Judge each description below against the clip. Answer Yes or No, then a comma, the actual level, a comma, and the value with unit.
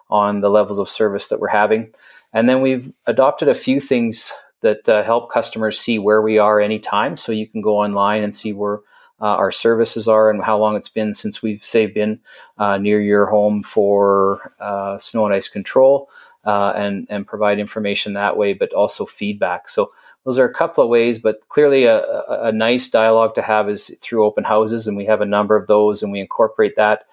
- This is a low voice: Yes, low, 105 Hz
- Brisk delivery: Yes, fast, 210 wpm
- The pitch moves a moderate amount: No, narrow, 1.5 semitones